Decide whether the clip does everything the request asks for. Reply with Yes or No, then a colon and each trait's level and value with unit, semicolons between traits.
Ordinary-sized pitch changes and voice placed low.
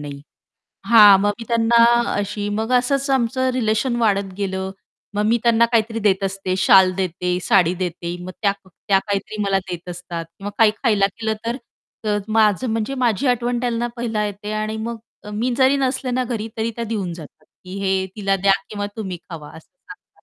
No: average, 3.4 semitones; high, 210 Hz